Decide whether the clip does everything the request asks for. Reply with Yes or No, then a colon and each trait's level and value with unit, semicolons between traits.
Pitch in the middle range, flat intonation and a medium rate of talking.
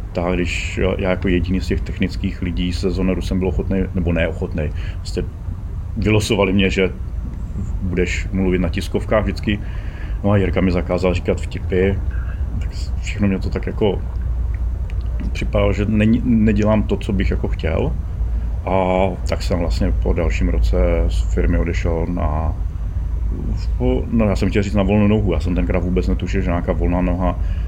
No: very low, 90 Hz; narrow, 2.2 semitones; average, 160 wpm